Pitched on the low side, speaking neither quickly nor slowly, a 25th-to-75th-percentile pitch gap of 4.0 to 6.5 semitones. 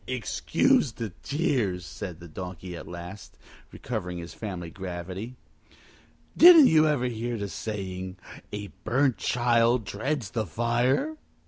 No: low, 110 Hz; slow, 125 wpm; wide, 5.4 semitones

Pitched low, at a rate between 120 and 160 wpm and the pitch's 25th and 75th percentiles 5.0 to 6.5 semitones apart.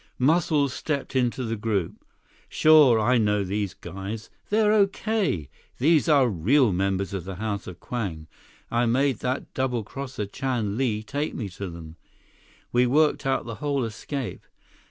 Yes: low, 120 Hz; average, 155 wpm; wide, 5.6 semitones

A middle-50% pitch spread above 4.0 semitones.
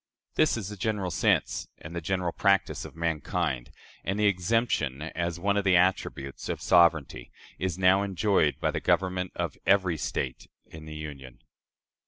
No: average, 3.7 semitones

